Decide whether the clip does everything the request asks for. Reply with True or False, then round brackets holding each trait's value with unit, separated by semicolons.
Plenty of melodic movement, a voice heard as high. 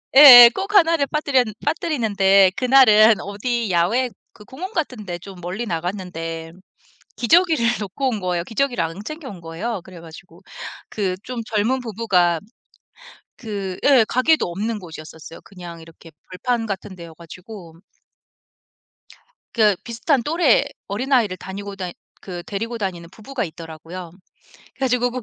True (5.8 semitones; 205 Hz)